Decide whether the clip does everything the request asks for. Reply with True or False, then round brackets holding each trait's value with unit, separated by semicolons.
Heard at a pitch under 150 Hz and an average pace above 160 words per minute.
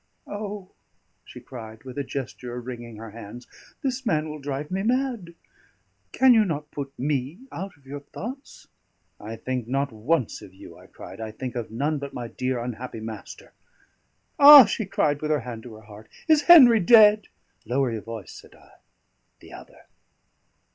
True (140 Hz; 175 wpm)